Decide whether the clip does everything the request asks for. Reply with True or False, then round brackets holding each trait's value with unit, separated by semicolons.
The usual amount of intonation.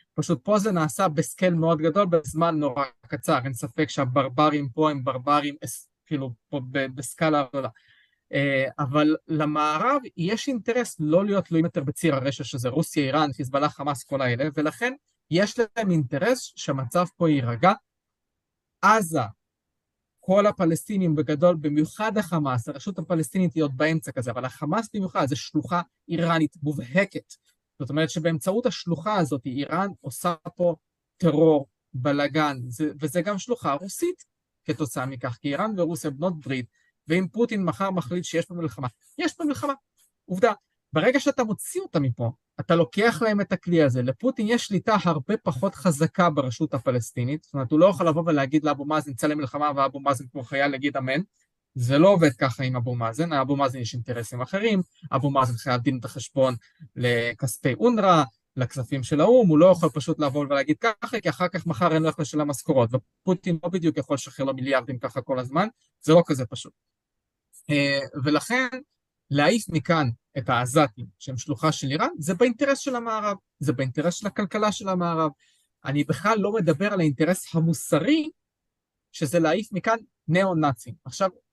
True (4.7 semitones)